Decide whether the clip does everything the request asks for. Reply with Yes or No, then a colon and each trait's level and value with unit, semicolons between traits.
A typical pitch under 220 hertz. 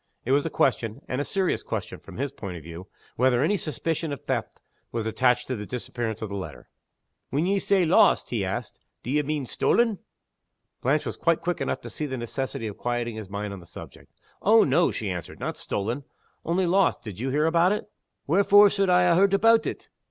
Yes: medium, 140 Hz